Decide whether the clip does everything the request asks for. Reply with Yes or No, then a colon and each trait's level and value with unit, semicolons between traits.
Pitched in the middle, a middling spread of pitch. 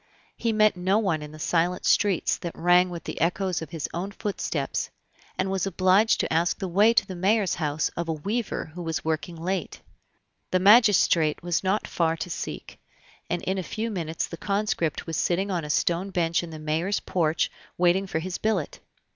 Yes: medium, 180 Hz; average, 3.0 semitones